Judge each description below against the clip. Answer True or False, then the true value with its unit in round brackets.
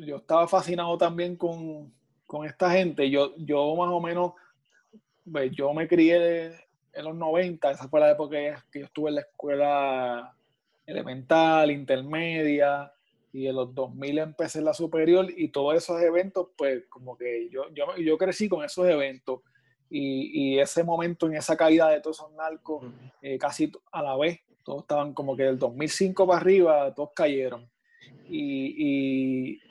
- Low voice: False (155 Hz)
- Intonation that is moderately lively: True (3.4 semitones)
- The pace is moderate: True (170 wpm)